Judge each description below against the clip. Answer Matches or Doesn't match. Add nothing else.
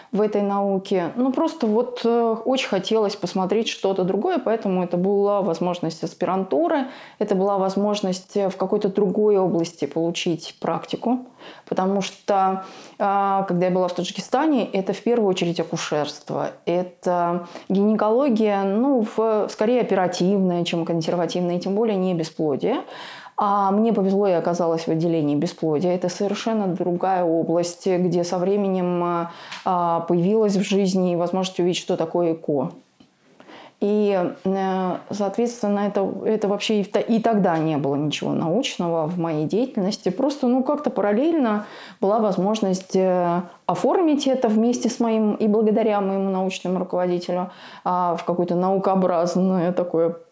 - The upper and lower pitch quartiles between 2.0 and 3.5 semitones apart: Matches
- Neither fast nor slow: Matches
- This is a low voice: Doesn't match